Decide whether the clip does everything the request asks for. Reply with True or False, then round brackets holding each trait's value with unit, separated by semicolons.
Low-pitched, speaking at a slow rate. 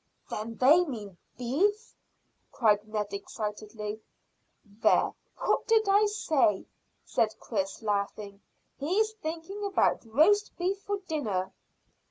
False (245 Hz; 110 wpm)